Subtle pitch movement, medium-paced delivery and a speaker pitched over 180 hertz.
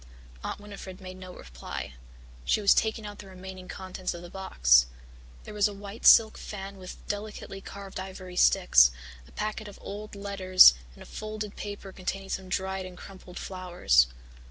Yes: narrow, 1.8 semitones; average, 170 wpm; high, 190 Hz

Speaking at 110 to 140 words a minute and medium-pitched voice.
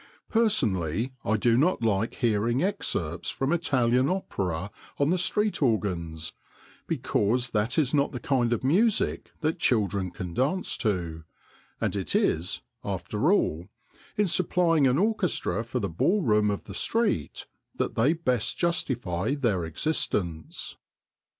No: slow, 135 wpm; low, 120 Hz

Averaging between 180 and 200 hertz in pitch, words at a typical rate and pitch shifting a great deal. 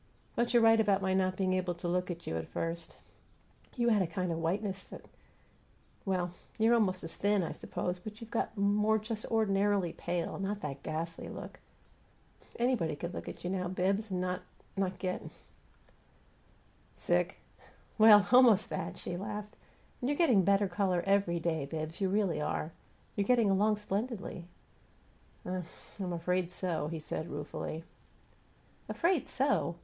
No: high, 190 Hz; average, 165 wpm; average, 3.3 semitones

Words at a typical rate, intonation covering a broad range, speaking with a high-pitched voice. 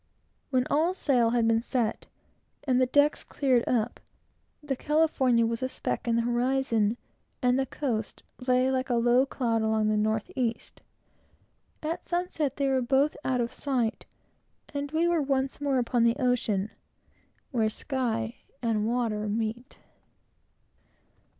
No: average, 145 wpm; average, 2.9 semitones; very high, 250 Hz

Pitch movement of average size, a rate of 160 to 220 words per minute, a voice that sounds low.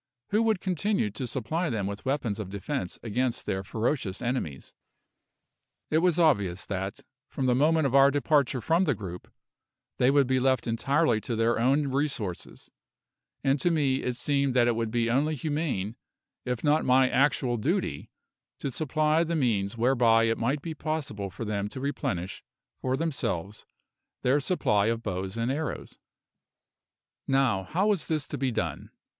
Yes: average, 5.0 semitones; average, 165 wpm; low, 130 Hz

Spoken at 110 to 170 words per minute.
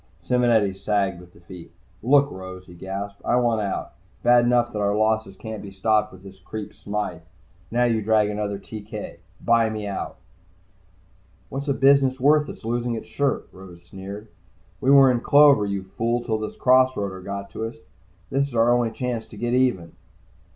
No: average, 185 wpm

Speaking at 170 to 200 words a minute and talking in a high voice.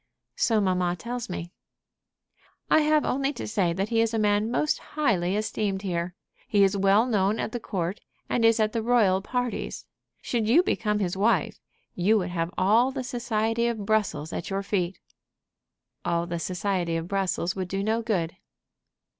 Yes: average, 175 wpm; high, 205 Hz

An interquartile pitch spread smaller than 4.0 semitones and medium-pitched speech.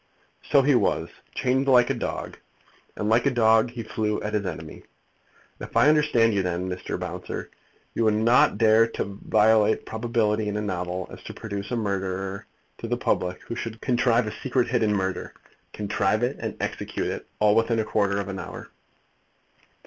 No: average, 2.9 semitones; low, 110 Hz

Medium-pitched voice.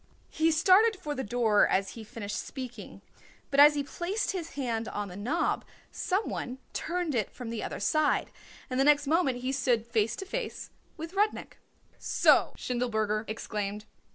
No: very high, 260 Hz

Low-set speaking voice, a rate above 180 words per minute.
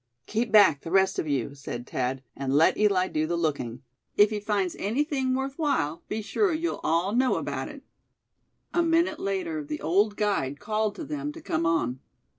No: high, 195 Hz; average, 190 wpm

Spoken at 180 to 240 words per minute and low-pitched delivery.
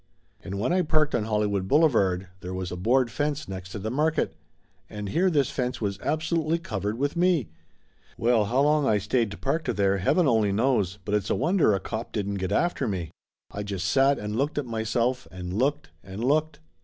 Yes: average, 200 wpm; low, 115 Hz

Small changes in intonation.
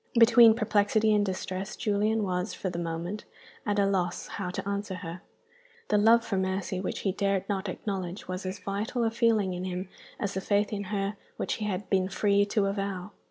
Yes: narrow, 2.1 semitones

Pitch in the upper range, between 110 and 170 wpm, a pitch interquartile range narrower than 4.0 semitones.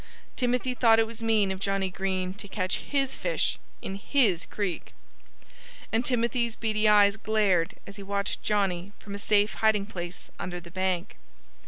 Yes: high, 205 Hz; average, 165 wpm; average, 2.9 semitones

